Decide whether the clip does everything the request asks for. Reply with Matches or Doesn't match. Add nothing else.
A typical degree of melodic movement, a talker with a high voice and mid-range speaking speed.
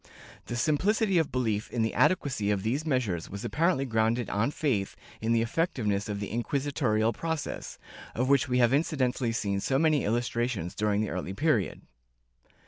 Doesn't match